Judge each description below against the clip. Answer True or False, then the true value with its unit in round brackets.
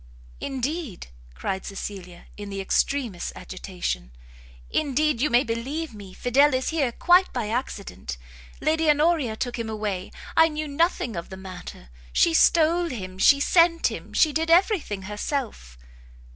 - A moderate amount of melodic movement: False (8.1 semitones)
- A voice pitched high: True (245 Hz)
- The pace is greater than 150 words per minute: False (145 wpm)